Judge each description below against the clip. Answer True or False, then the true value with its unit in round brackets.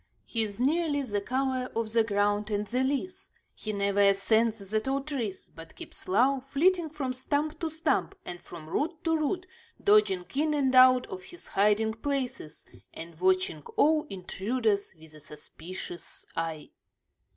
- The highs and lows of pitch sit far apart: True (5.9 semitones)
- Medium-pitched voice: False (225 Hz)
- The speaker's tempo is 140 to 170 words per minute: True (160 wpm)